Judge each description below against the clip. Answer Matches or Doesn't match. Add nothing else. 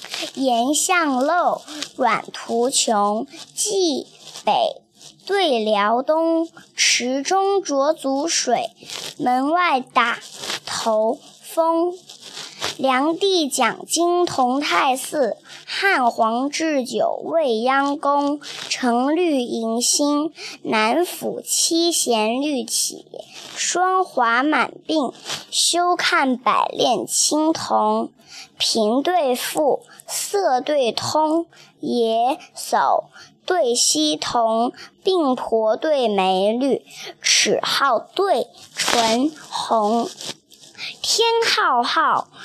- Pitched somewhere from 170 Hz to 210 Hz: Doesn't match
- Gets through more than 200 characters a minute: Doesn't match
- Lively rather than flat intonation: Matches